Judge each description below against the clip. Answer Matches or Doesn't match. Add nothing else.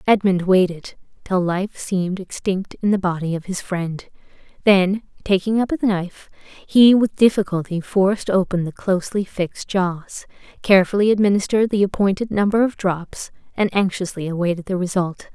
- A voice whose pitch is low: Doesn't match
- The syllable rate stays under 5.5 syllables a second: Matches